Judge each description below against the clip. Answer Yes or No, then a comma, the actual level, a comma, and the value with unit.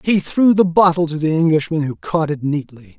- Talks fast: Yes, fast, 220 wpm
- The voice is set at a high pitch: No, medium, 160 Hz